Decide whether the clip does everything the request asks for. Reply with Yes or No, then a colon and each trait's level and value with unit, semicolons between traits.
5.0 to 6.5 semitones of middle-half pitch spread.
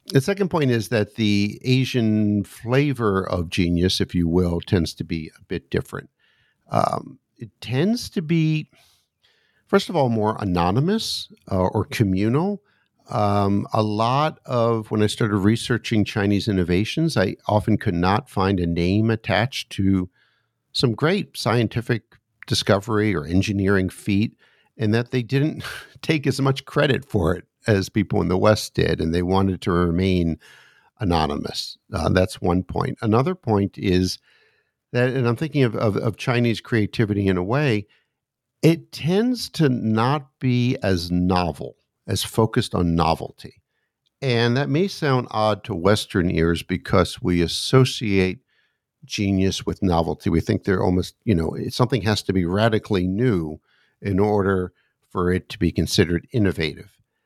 Yes: average, 5.3 semitones